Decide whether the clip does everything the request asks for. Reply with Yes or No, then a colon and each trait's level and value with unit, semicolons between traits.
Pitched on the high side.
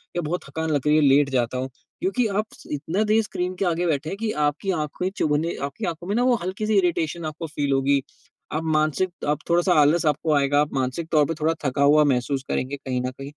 No: medium, 155 Hz